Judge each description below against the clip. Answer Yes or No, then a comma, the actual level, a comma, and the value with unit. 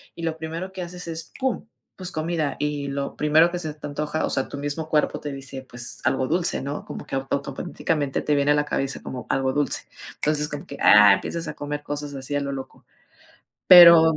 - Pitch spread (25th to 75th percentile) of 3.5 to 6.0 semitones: No, average, 2.8 semitones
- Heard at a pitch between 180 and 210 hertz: No, medium, 150 Hz